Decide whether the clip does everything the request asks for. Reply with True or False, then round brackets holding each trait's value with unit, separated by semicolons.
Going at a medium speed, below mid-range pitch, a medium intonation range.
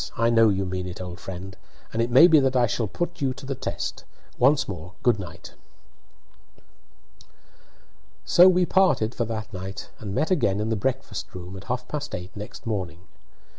False (185 wpm; 110 Hz; 5.7 semitones)